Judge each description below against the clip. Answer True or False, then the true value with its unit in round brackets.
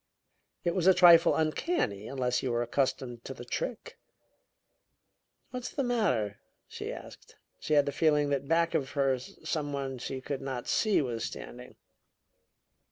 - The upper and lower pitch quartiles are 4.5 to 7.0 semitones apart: True (5.0 semitones)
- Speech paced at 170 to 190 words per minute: False (155 wpm)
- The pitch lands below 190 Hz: True (140 Hz)